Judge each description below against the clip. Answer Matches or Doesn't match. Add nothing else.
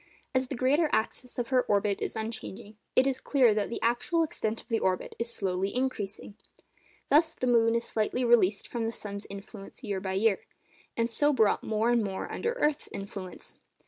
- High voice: Matches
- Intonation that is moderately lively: Matches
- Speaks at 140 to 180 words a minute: Doesn't match